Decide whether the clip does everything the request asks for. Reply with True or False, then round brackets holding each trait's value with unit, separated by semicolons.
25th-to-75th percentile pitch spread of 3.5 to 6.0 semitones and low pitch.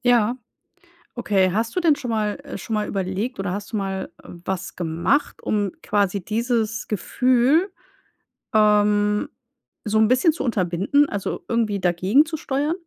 False (4.1 semitones; 215 Hz)